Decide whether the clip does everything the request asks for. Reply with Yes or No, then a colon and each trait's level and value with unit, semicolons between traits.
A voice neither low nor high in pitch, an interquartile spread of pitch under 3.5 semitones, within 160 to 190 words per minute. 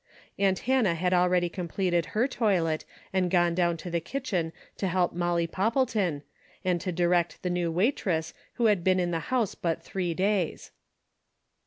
Yes: medium, 180 Hz; narrow, 2.4 semitones; average, 165 wpm